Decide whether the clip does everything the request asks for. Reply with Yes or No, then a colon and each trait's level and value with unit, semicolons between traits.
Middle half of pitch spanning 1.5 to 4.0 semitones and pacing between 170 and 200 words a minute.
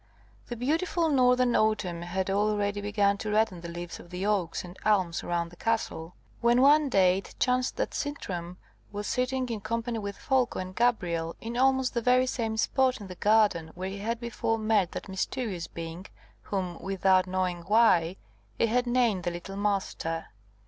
No: average, 4.7 semitones; average, 175 wpm